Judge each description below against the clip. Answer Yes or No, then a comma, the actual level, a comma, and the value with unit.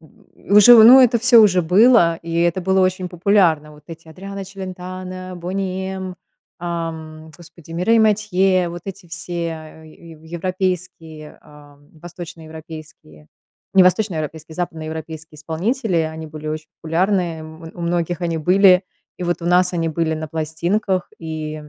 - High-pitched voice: No, medium, 175 Hz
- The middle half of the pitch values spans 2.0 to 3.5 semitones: Yes, average, 2.8 semitones